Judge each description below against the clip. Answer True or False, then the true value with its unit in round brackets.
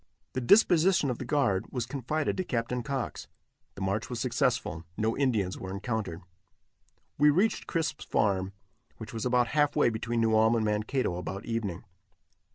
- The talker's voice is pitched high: False (115 Hz)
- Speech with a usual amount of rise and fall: True (4.3 semitones)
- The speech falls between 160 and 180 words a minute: True (165 wpm)